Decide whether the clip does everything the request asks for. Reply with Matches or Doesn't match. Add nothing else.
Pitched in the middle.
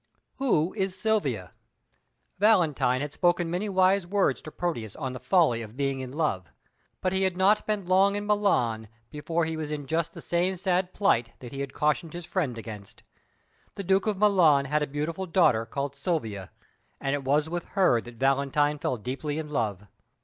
Matches